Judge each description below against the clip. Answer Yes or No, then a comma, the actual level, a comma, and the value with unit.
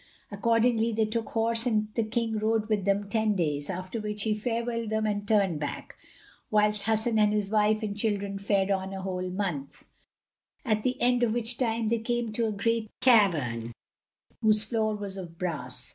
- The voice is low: No, high, 215 Hz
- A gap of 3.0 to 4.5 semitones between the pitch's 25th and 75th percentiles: No, narrow, 2.4 semitones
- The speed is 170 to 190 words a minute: Yes, average, 185 wpm